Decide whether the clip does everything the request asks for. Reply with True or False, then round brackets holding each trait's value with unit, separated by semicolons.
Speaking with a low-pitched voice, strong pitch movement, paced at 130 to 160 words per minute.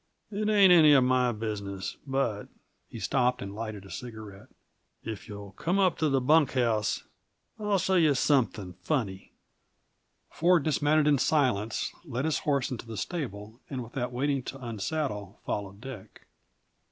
True (125 Hz; 6.1 semitones; 155 wpm)